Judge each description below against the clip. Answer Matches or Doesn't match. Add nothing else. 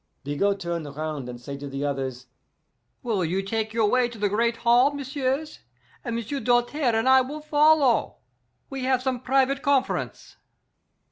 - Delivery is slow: Doesn't match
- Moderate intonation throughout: Doesn't match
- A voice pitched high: Matches